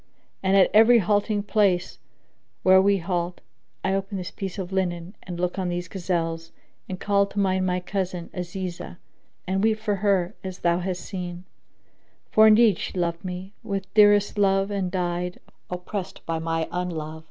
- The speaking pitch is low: No, medium, 185 Hz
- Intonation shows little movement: Yes, narrow, 2.1 semitones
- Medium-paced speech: Yes, average, 165 wpm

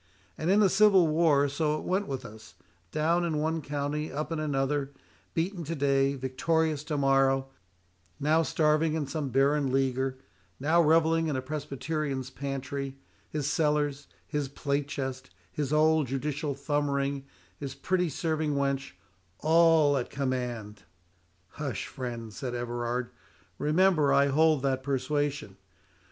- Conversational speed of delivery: No, slow, 130 wpm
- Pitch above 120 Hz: Yes, medium, 140 Hz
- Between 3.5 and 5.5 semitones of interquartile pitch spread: No, narrow, 2.6 semitones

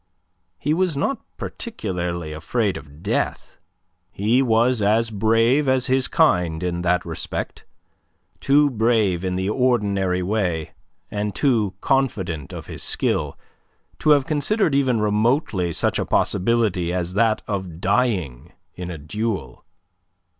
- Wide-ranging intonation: Yes, wide, 5.9 semitones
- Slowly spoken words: Yes, slow, 130 wpm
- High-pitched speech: No, low, 105 Hz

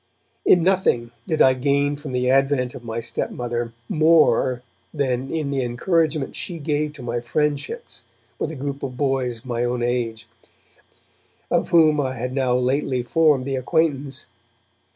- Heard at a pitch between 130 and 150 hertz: Yes, low, 135 Hz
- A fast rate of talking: No, average, 155 wpm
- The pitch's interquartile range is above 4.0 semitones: No, average, 3.3 semitones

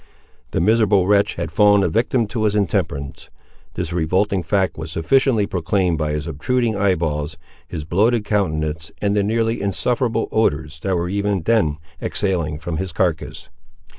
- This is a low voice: Yes, very low, 95 Hz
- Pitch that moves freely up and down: No, average, 4.6 semitones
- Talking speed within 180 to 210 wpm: No, average, 160 wpm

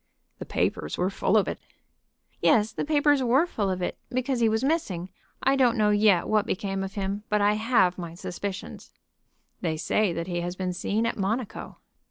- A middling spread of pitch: Yes, average, 4.0 semitones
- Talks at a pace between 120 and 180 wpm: No, average, 195 wpm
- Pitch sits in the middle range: No, high, 205 Hz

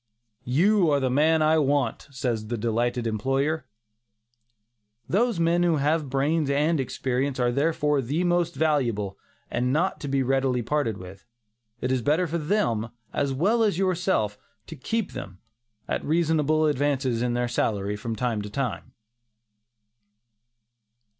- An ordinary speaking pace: Yes, average, 145 wpm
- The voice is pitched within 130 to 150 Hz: Yes, medium, 140 Hz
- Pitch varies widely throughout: No, average, 4.8 semitones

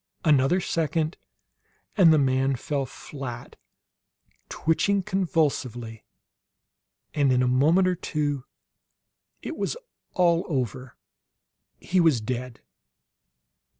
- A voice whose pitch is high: No, medium, 145 Hz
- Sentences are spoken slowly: Yes, slow, 95 wpm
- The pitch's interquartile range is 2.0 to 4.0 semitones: No, average, 4.6 semitones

